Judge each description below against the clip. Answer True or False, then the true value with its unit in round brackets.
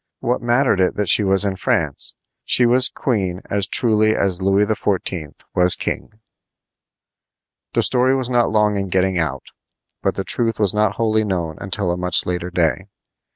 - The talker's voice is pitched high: False (100 Hz)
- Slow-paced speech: False (170 wpm)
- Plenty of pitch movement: False (3.4 semitones)